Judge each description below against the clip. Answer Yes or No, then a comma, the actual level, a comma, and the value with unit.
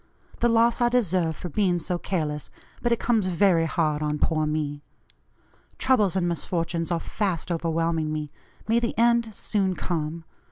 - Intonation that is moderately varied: Yes, average, 5.0 semitones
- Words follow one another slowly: No, average, 160 wpm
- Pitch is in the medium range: Yes, medium, 175 Hz